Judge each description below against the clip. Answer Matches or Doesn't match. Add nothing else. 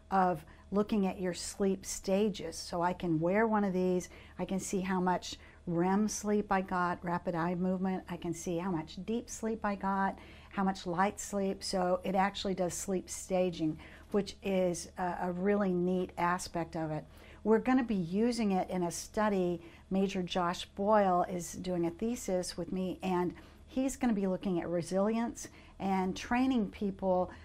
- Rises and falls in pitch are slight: Matches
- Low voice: Doesn't match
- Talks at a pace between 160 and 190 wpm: Matches